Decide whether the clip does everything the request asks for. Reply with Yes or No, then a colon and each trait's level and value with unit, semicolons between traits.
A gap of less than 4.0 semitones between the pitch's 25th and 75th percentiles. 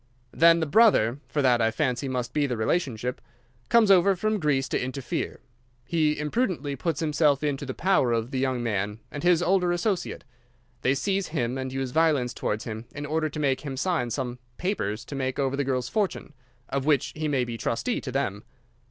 No: average, 4.5 semitones